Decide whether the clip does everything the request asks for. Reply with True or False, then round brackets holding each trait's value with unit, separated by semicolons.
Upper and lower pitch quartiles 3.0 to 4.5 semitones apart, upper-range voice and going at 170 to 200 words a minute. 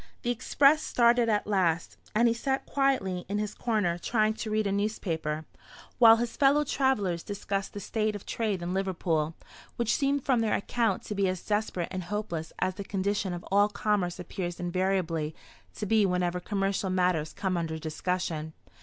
True (3.6 semitones; 200 Hz; 175 wpm)